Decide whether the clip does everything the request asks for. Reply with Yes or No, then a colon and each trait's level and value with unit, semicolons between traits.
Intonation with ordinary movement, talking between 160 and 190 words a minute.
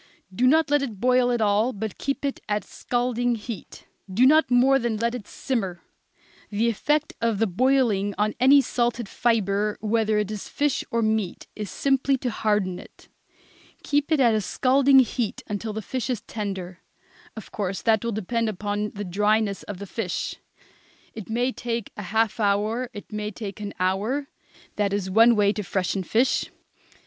Yes: average, 3.3 semitones; average, 180 wpm